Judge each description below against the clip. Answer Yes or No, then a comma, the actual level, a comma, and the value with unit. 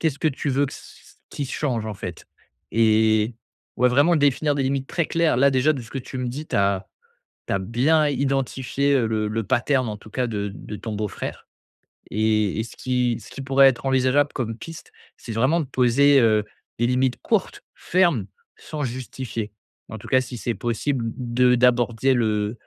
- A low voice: Yes, low, 125 Hz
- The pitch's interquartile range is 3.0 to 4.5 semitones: Yes, average, 3.7 semitones